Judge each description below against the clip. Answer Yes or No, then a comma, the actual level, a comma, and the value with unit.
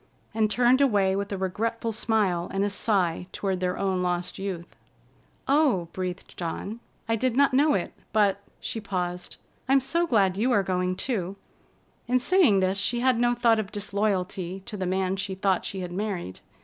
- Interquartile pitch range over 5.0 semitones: No, average, 3.7 semitones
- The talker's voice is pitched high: Yes, high, 200 Hz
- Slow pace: No, average, 175 wpm